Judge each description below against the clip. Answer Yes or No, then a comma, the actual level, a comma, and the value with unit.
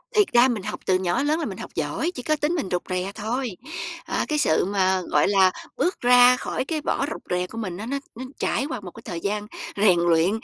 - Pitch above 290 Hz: No, high, 210 Hz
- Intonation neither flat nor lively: No, wide, 6.4 semitones